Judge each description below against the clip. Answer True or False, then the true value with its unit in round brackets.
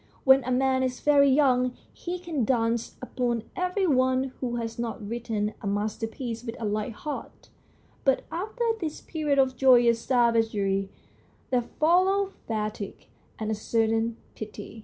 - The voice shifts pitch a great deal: False (3.4 semitones)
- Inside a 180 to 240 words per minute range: False (145 wpm)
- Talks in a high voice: True (245 Hz)